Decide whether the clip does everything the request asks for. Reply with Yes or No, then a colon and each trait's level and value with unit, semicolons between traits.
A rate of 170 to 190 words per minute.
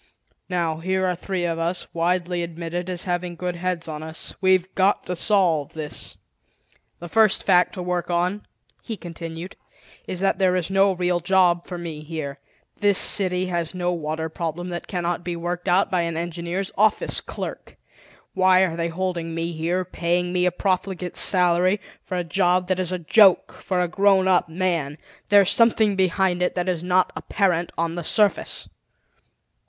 Yes: average, 175 wpm